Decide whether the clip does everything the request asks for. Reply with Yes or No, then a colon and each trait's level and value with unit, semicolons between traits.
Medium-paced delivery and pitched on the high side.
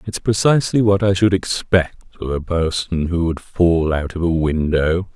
No: average, 185 wpm; very low, 90 Hz